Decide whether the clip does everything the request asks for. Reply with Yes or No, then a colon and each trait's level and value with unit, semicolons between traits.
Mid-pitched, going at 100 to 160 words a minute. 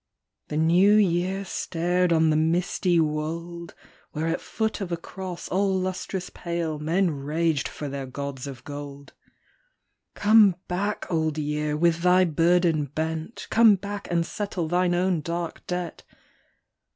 Yes: medium, 170 Hz; average, 150 wpm